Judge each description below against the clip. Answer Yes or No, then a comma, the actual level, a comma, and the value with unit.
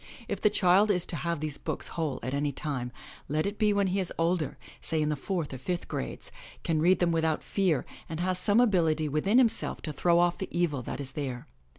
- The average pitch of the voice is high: No, medium, 165 Hz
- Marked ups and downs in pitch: No, average, 3.8 semitones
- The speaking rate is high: Yes, fast, 230 wpm